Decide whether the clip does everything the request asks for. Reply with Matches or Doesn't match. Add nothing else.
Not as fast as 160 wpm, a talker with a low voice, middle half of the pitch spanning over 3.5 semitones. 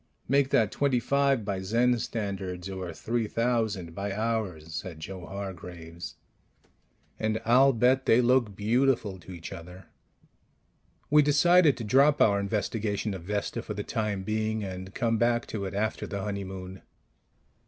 Matches